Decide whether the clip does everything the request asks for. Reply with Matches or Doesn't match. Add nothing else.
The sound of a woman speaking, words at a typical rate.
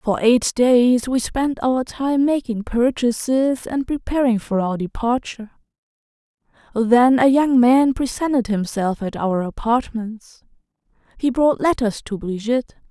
Doesn't match